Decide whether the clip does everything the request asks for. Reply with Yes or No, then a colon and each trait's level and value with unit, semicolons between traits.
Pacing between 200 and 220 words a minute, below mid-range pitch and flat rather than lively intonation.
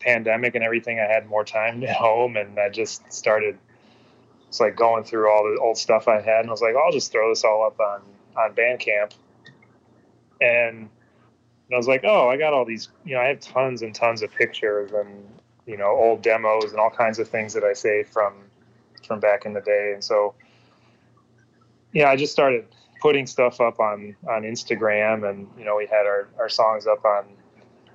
Yes: fast, 205 wpm; low, 115 Hz; narrow, 2.3 semitones